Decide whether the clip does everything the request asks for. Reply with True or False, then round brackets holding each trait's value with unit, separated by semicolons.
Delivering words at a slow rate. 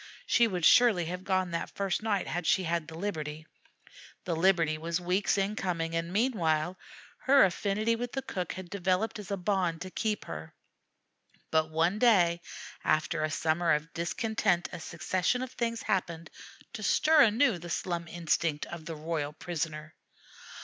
False (165 wpm)